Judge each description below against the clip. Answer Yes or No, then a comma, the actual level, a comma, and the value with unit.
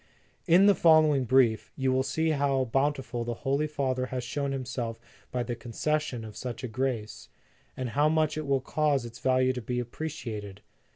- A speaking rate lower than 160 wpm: No, average, 180 wpm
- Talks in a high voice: No, low, 130 Hz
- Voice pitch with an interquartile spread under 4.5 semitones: Yes, average, 3.4 semitones